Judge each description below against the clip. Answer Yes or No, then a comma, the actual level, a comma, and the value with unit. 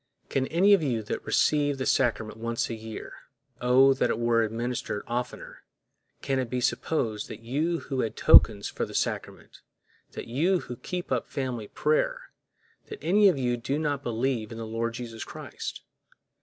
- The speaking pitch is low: Yes, low, 125 Hz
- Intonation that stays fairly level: No, average, 4.0 semitones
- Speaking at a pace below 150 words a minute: No, average, 170 wpm